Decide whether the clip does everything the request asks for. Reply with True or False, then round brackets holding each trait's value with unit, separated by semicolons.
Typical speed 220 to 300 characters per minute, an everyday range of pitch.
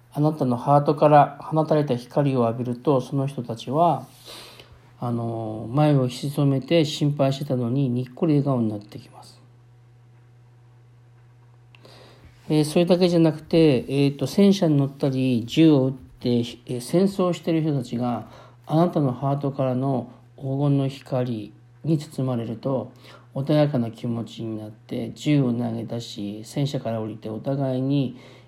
True (290 characters per minute; 3.1 semitones)